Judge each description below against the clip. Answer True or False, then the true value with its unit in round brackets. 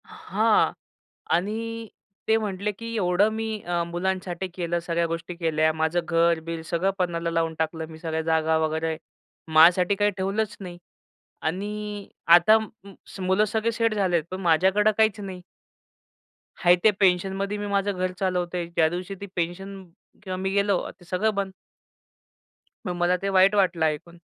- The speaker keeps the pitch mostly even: False (3.0 semitones)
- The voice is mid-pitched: True (180 Hz)